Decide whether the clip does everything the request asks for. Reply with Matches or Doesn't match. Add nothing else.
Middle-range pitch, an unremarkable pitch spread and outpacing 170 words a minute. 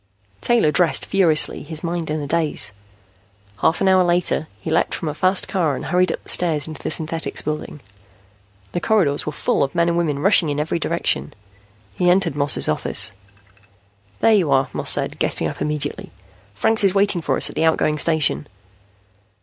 Matches